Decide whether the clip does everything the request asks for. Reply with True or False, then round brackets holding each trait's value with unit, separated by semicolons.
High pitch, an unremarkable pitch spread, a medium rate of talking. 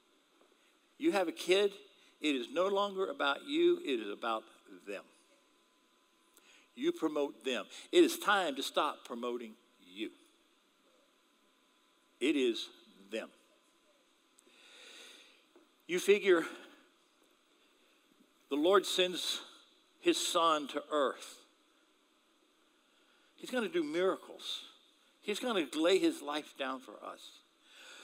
False (330 Hz; 3.6 semitones; 105 wpm)